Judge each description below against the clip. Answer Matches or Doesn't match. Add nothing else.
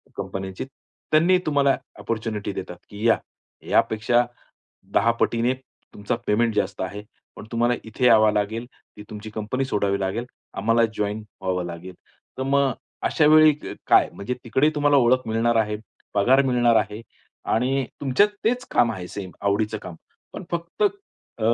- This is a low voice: Matches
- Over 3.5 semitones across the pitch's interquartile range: Matches